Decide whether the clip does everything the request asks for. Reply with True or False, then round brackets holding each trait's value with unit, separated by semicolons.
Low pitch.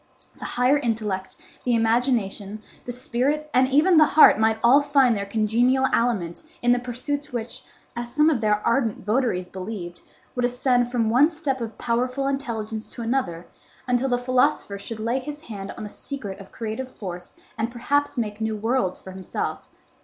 False (240 Hz)